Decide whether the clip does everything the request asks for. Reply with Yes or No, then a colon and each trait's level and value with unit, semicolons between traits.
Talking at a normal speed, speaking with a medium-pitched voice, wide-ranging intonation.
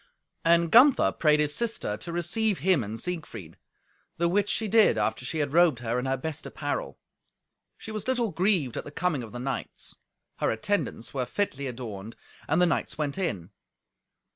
Yes: average, 180 wpm; medium, 160 Hz; wide, 7.2 semitones